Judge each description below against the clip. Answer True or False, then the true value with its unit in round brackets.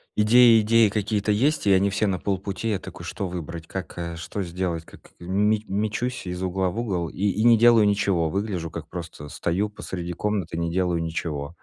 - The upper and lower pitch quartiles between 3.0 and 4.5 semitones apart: True (3.7 semitones)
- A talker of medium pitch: False (95 Hz)